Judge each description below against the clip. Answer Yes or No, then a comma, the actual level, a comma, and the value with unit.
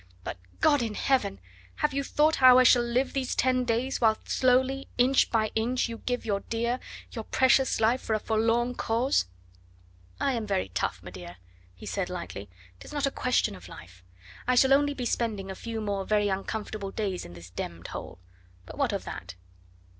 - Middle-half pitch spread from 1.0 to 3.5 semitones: No, average, 4.4 semitones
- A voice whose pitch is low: No, high, 230 Hz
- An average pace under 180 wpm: No, average, 190 wpm